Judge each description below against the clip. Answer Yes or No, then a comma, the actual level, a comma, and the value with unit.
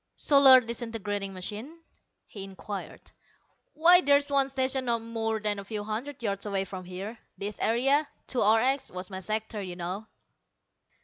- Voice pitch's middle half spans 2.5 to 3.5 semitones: No, average, 4.8 semitones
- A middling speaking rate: Yes, average, 150 wpm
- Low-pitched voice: No, high, 220 Hz